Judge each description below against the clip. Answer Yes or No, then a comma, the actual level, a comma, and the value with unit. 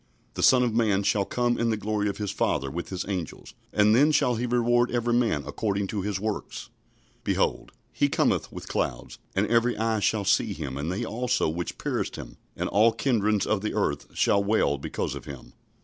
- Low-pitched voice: Yes, low, 105 Hz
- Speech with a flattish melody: No, average, 3.4 semitones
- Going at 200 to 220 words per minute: Yes, fast, 205 wpm